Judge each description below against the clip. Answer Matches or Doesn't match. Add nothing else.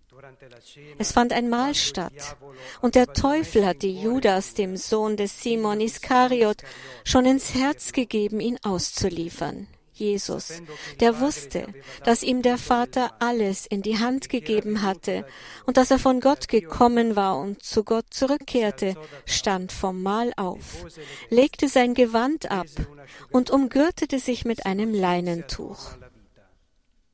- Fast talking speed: Doesn't match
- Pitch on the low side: Doesn't match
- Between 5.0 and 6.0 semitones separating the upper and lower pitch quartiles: Matches